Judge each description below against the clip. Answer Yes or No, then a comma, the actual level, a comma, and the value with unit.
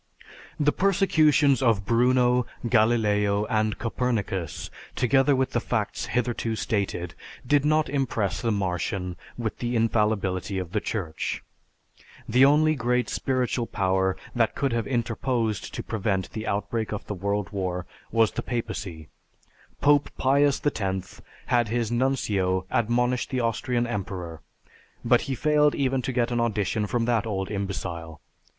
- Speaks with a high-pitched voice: No, low, 115 Hz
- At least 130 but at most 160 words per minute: Yes, average, 140 wpm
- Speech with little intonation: No, average, 4.1 semitones